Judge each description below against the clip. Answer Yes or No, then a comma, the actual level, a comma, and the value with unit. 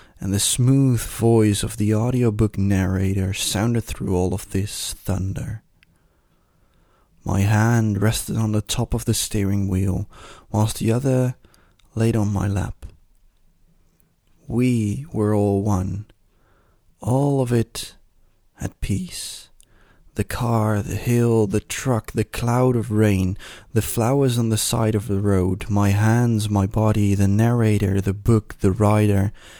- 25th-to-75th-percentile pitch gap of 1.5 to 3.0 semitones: Yes, average, 2.7 semitones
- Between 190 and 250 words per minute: No, average, 140 wpm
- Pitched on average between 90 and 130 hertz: Yes, low, 105 Hz